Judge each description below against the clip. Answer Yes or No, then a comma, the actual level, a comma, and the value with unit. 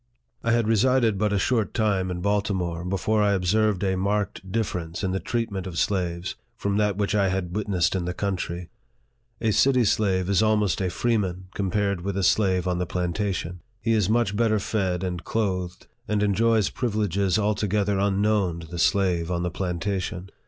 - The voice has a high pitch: No, low, 100 Hz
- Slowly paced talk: No, average, 180 wpm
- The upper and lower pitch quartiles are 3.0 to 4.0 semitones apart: No, narrow, 2.6 semitones